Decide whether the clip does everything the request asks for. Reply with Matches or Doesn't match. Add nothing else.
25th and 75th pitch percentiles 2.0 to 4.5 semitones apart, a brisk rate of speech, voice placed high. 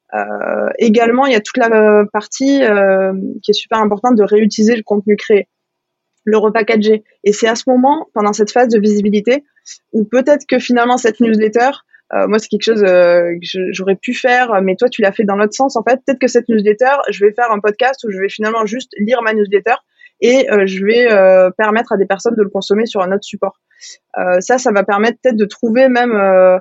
Matches